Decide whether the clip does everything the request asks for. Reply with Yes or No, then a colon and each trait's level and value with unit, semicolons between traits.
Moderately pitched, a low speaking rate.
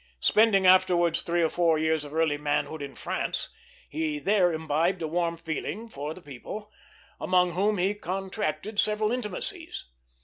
No: medium, 175 Hz; average, 150 wpm